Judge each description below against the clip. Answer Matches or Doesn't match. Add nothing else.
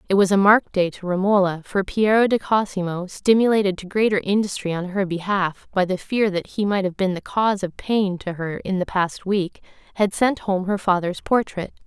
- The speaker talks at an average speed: Doesn't match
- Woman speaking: Matches